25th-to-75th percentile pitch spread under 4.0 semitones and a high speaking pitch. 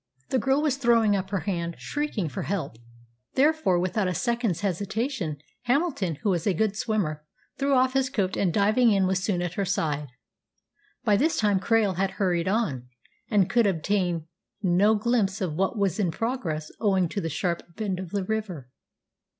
No: average, 4.3 semitones; high, 200 Hz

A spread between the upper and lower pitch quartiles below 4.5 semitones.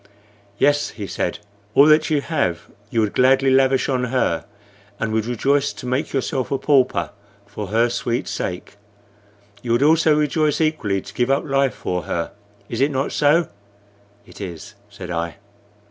No: average, 5.1 semitones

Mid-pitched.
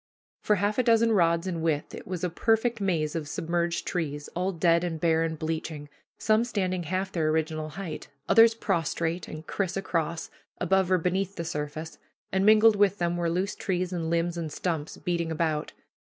Yes: medium, 170 Hz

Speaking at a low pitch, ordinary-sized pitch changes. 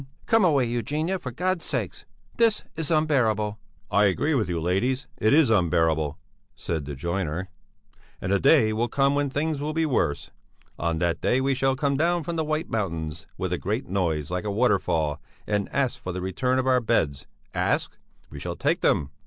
No: low, 115 Hz; wide, 8.6 semitones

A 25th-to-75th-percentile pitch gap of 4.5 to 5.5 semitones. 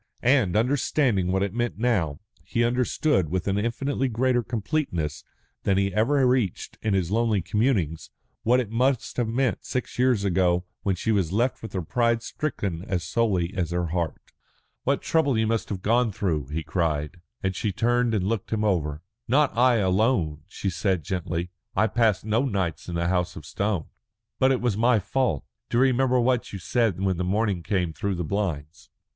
Yes: average, 5.2 semitones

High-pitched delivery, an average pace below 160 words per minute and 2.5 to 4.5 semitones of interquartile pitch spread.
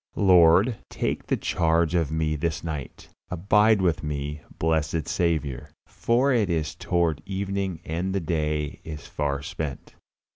No: very low, 80 Hz; average, 140 wpm; average, 3.5 semitones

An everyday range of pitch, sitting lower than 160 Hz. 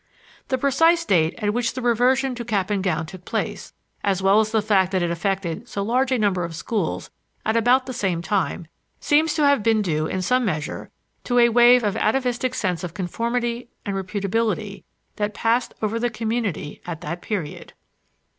No: average, 4.6 semitones; high, 215 Hz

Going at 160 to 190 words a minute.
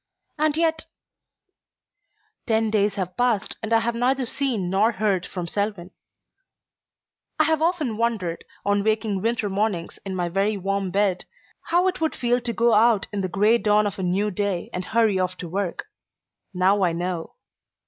Yes: average, 170 wpm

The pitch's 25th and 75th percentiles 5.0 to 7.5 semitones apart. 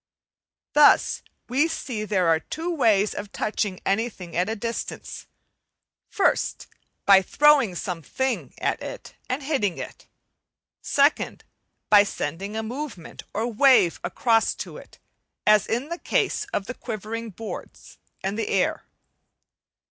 Yes: average, 5.3 semitones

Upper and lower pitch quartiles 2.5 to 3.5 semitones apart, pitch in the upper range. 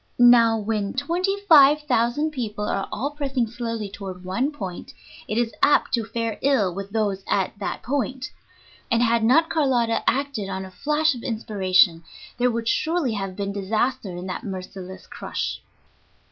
No: average, 5.2 semitones; high, 230 Hz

